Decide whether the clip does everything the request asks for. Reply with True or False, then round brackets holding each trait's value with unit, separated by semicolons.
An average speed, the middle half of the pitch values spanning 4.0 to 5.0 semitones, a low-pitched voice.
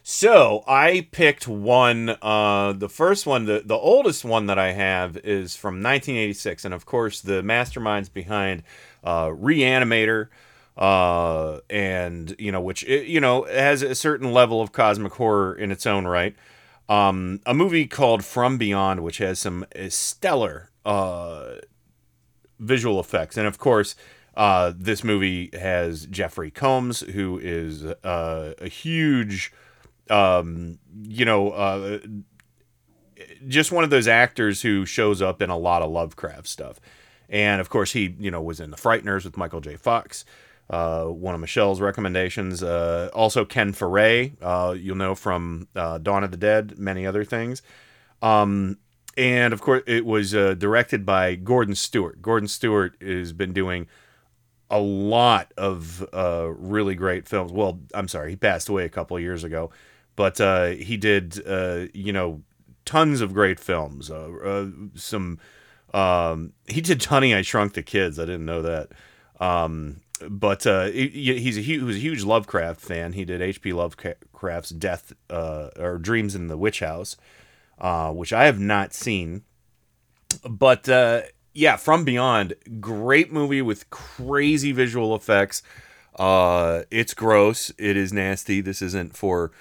True (155 wpm; 4.4 semitones; 100 Hz)